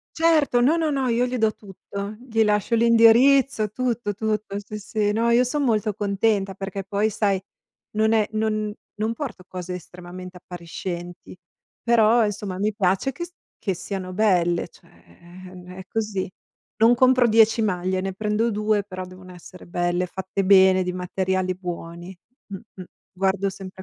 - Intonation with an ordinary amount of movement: Yes, average, 3.3 semitones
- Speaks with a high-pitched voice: Yes, high, 205 Hz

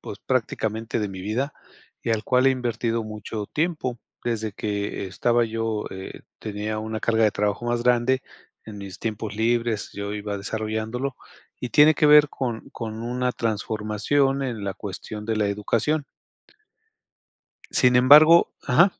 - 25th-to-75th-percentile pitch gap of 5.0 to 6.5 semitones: No, average, 3.0 semitones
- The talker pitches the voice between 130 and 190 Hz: No, low, 115 Hz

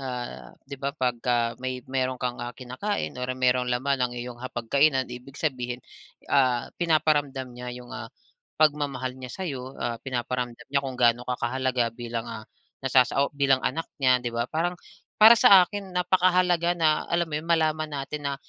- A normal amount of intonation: Yes, average, 3.7 semitones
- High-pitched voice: No, low, 130 Hz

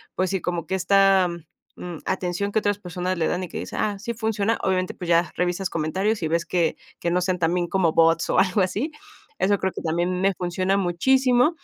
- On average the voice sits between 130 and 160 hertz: No, medium, 185 Hz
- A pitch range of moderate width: No, narrow, 2.2 semitones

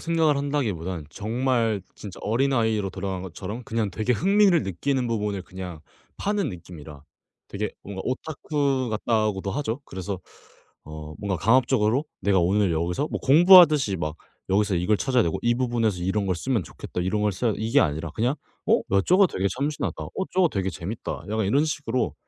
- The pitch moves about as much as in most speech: No, wide, 5.9 semitones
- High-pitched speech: No, low, 110 Hz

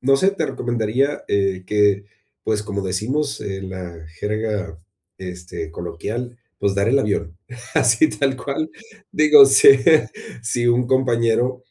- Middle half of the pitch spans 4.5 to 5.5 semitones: Yes, average, 5.1 semitones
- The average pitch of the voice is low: Yes, low, 110 Hz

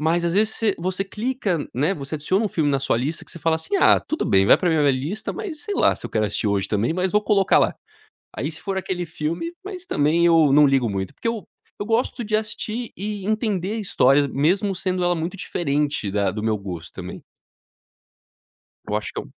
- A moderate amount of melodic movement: No, wide, 7.1 semitones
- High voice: No, medium, 170 Hz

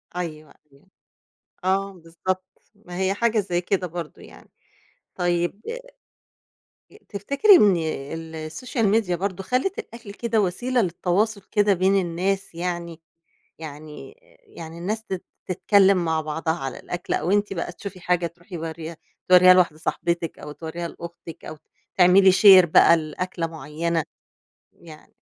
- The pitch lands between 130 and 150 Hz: No, medium, 180 Hz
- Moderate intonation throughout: Yes, average, 3.0 semitones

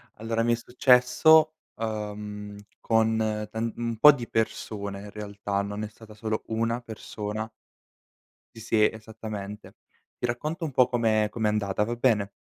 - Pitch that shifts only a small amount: Yes, narrow, 1.9 semitones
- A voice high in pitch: No, low, 110 Hz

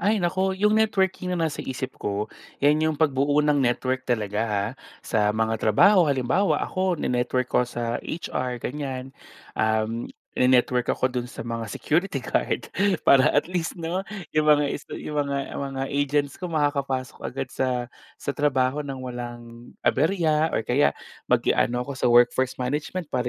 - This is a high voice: No, low, 135 Hz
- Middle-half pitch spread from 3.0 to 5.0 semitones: Yes, average, 4.0 semitones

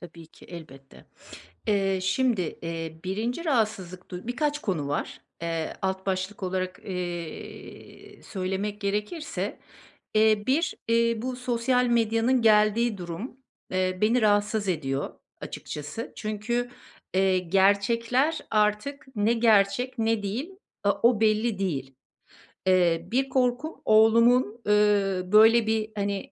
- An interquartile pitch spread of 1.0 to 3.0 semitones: No, average, 4.0 semitones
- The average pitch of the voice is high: Yes, high, 210 Hz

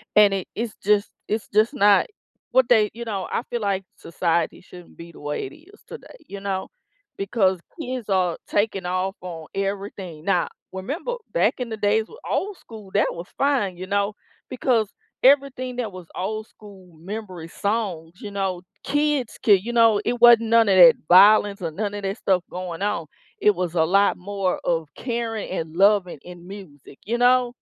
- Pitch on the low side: No, high, 200 Hz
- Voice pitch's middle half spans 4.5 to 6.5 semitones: No, average, 3.8 semitones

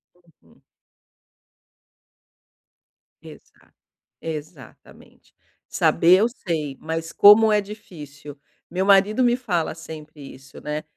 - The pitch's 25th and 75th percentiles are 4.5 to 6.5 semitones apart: Yes, average, 5.2 semitones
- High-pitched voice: No, medium, 165 Hz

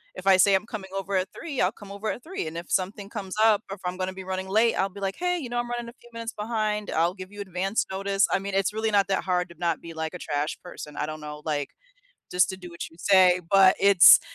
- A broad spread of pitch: No, narrow, 2.6 semitones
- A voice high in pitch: Yes, high, 195 Hz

